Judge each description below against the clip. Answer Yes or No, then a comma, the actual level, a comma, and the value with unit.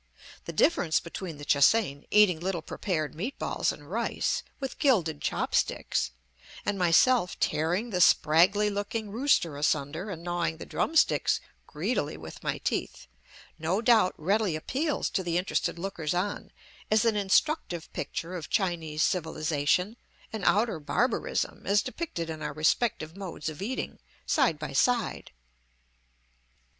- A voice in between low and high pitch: Yes, medium, 180 Hz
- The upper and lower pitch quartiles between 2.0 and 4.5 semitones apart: No, average, 5.2 semitones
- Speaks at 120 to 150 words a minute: Yes, average, 140 wpm